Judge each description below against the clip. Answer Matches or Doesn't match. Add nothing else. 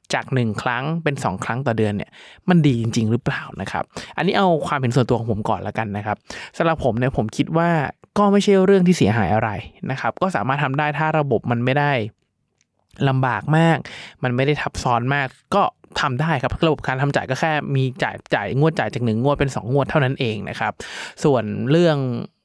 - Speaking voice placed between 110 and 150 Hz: Matches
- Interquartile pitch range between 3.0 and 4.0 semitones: Doesn't match